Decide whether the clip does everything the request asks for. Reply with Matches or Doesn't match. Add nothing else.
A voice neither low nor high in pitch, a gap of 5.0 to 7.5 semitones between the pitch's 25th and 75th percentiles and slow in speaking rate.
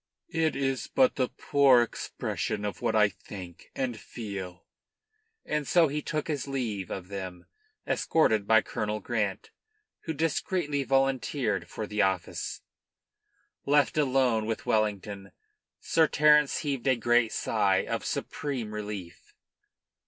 Doesn't match